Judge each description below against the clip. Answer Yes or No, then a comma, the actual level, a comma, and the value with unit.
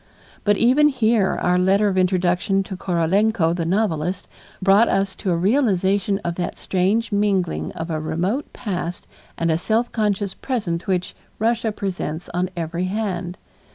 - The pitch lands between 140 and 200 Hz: Yes, high, 190 Hz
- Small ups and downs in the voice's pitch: No, average, 3.2 semitones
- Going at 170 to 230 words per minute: No, average, 155 wpm